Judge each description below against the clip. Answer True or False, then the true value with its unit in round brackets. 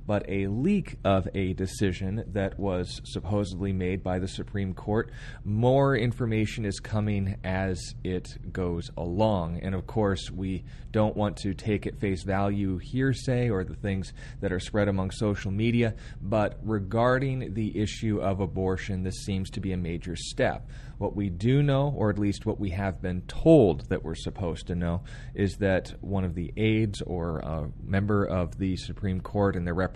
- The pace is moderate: True (180 wpm)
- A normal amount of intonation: True (3.0 semitones)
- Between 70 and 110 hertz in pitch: True (100 Hz)